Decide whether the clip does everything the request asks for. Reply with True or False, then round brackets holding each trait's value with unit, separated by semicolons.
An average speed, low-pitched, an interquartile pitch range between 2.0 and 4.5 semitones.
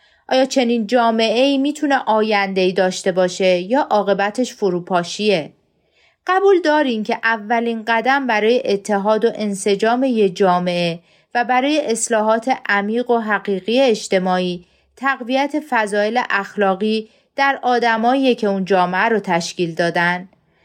False (115 wpm; 220 Hz; 4.1 semitones)